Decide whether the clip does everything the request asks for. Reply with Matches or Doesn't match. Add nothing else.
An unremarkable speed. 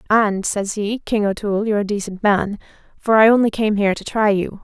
Doesn't match